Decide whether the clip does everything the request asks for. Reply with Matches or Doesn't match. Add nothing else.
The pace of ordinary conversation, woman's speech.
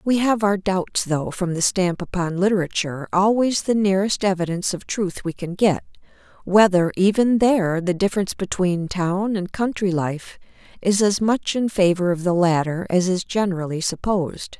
Matches